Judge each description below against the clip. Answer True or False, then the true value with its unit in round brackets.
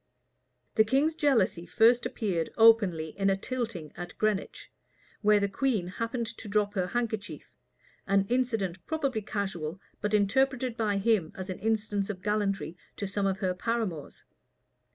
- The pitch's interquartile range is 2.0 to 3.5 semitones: True (3.2 semitones)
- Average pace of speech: True (150 wpm)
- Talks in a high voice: True (210 Hz)